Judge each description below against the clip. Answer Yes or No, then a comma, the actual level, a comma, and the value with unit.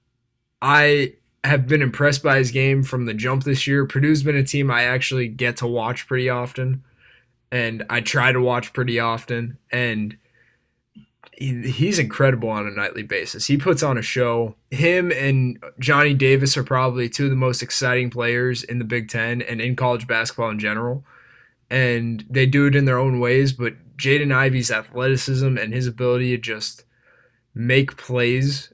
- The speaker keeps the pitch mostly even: Yes, narrow, 2.1 semitones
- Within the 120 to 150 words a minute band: No, average, 175 wpm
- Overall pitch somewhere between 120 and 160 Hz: Yes, low, 125 Hz